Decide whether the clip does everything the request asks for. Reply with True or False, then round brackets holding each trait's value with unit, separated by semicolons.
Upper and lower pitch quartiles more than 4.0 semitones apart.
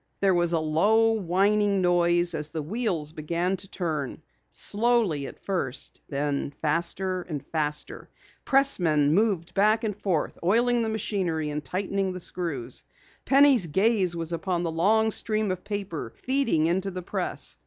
True (4.6 semitones)